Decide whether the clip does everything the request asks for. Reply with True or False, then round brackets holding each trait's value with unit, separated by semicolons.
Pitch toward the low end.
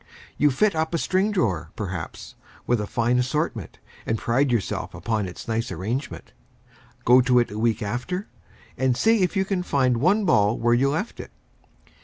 True (125 Hz)